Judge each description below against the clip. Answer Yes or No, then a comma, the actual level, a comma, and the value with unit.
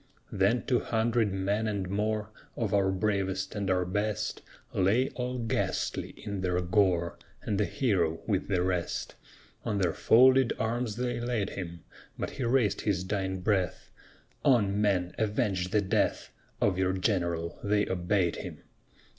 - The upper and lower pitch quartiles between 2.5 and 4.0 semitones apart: Yes, average, 2.9 semitones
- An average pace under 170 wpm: Yes, average, 150 wpm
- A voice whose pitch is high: No, low, 100 Hz